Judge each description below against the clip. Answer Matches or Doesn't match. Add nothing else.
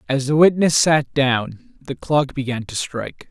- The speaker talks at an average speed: Matches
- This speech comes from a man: Matches